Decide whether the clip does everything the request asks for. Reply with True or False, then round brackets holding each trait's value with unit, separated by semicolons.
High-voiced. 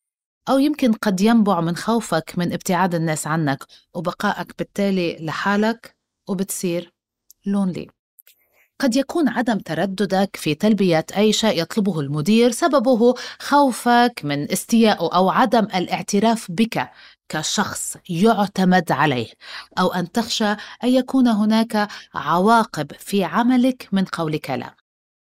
True (200 Hz)